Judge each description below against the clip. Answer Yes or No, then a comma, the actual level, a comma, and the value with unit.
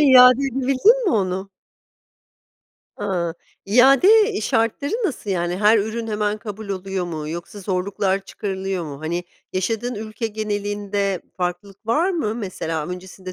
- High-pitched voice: Yes, high, 205 Hz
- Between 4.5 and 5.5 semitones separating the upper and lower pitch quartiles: No, average, 3.6 semitones